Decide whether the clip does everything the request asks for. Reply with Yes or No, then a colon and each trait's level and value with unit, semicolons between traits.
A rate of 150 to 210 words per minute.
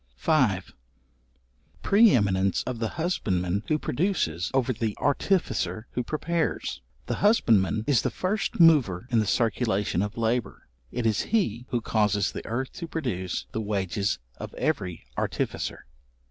No: average, 140 wpm